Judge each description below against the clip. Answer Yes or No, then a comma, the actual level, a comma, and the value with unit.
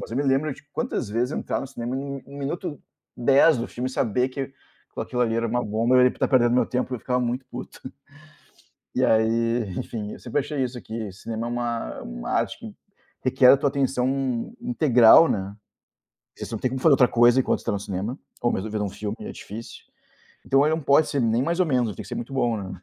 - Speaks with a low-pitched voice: Yes, low, 125 Hz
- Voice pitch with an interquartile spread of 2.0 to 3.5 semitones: Yes, average, 3.0 semitones